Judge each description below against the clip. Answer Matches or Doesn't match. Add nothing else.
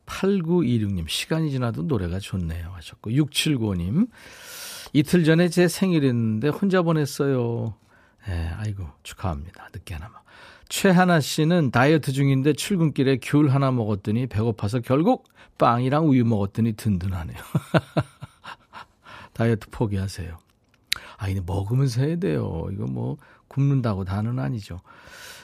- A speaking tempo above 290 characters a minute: Doesn't match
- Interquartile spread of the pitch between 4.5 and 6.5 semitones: Doesn't match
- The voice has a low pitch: Matches